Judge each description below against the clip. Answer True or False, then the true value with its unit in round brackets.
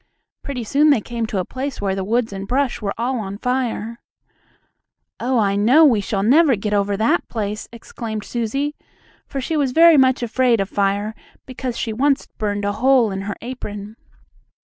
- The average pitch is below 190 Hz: False (230 Hz)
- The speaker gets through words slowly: False (185 wpm)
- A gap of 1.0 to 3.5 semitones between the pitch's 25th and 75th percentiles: False (4.2 semitones)